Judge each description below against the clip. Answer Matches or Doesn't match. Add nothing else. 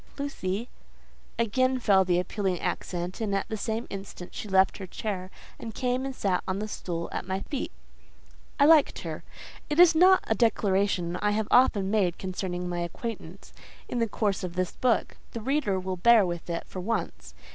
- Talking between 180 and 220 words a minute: Matches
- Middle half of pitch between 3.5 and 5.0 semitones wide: Matches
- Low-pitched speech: Doesn't match